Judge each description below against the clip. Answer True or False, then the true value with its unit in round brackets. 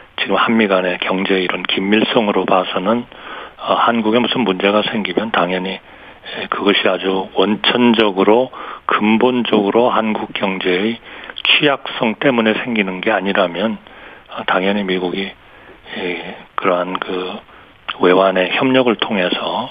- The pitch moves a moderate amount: True (3.2 semitones)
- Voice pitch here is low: True (100 Hz)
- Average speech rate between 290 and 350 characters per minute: False (270 characters per minute)